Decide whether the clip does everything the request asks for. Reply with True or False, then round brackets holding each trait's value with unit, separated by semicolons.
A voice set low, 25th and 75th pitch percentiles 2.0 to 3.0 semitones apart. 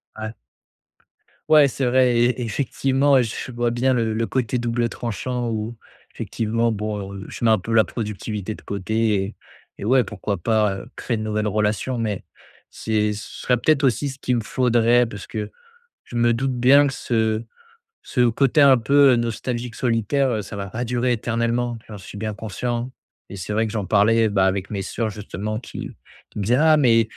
True (115 Hz; 2.5 semitones)